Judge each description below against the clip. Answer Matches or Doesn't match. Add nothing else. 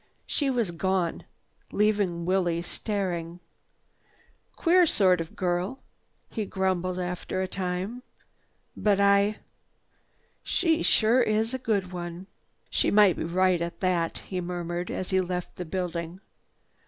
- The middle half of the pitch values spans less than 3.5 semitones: Matches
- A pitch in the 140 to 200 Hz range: Matches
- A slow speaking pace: Matches